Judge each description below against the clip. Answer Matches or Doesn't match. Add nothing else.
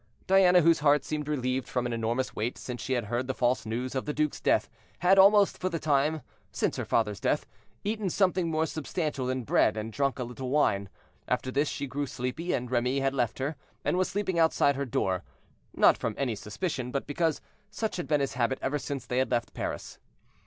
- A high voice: Doesn't match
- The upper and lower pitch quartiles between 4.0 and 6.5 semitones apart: Matches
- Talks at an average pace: Doesn't match